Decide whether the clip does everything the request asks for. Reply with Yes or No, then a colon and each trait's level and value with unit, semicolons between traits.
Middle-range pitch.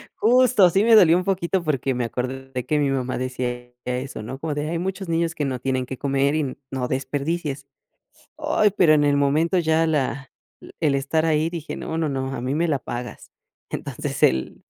Yes: medium, 145 Hz